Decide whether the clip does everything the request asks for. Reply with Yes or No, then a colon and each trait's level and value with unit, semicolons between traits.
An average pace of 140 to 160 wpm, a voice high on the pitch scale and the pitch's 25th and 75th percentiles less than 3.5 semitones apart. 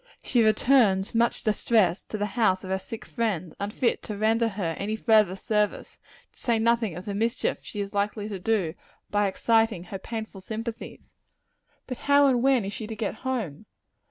No: average, 185 wpm; high, 215 Hz; average, 2.7 semitones